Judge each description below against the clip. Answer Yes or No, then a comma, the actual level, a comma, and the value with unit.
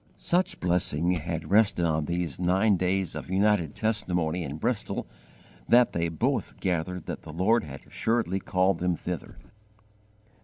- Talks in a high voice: No, very low, 90 Hz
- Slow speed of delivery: No, average, 145 wpm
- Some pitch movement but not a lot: Yes, average, 3.0 semitones